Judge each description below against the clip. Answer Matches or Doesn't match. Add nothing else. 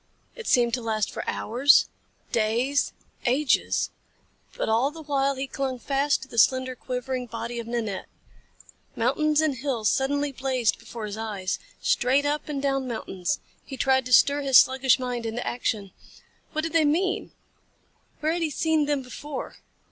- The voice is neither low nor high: Doesn't match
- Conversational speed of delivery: Matches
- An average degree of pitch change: Matches